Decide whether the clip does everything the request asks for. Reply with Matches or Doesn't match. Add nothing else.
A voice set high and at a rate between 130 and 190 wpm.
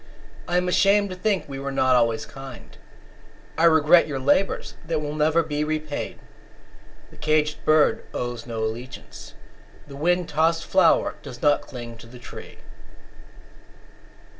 Doesn't match